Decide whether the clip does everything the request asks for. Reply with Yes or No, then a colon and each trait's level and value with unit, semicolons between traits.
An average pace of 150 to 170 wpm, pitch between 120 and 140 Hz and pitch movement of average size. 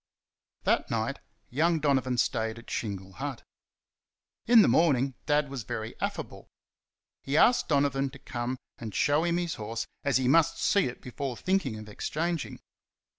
Yes: average, 155 wpm; low, 135 Hz; average, 4.6 semitones